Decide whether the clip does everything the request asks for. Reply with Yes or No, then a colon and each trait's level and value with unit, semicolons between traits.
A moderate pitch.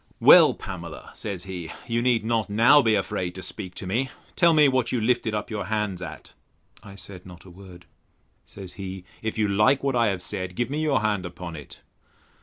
No: low, 105 Hz